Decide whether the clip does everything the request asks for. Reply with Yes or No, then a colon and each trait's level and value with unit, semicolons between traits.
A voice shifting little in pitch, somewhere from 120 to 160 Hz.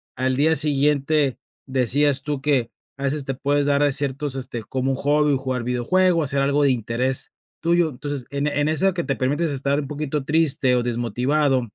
Yes: narrow, 2.3 semitones; medium, 140 Hz